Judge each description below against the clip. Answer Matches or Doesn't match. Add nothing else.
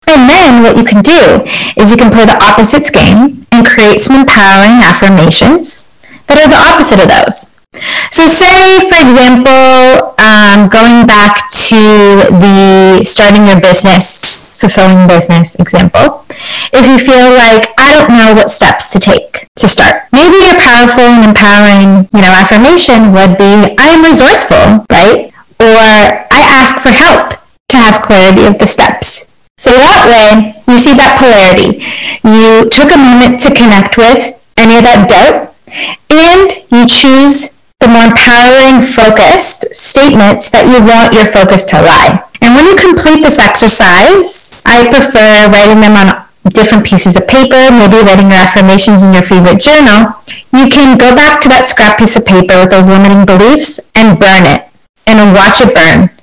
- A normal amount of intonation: Matches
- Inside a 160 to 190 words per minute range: Matches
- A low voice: Doesn't match